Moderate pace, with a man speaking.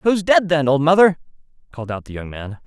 No: fast, 225 wpm; male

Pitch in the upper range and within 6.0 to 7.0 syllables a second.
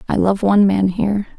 Yes: high, 195 Hz; 6.3 syllables/s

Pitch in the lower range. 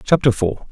Yes: low, 115 Hz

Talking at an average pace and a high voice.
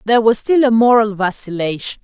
Yes: average, 175 wpm; high, 220 Hz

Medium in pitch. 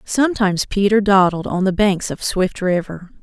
No: high, 195 Hz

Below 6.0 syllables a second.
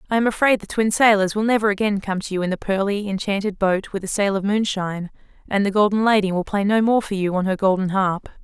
No: 6.2 syllables/s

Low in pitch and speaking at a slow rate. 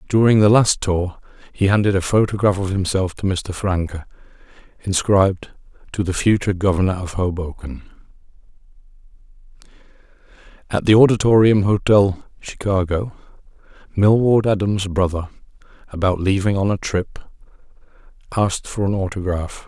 Yes: very low, 95 Hz; slow, 115 wpm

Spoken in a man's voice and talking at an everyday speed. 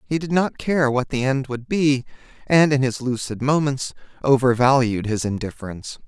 Yes: male; average, 170 wpm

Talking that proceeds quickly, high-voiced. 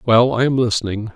No: fast, 210 wpm; low, 115 Hz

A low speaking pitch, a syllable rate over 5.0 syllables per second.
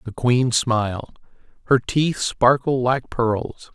No: low, 125 Hz; 3.2 syllables/s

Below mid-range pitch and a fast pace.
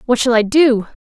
No: high, 240 Hz; fast, 230 wpm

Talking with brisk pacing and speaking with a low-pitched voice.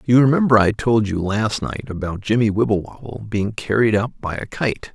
No: average, 195 wpm; low, 110 Hz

